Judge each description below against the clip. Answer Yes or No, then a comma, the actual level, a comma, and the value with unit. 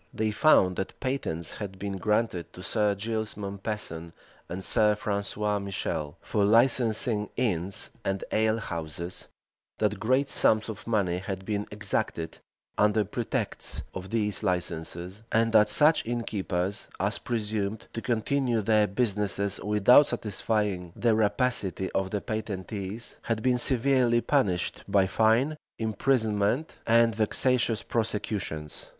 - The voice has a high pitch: No, low, 105 Hz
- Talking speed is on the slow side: Yes, slow, 125 wpm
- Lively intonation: No, average, 2.8 semitones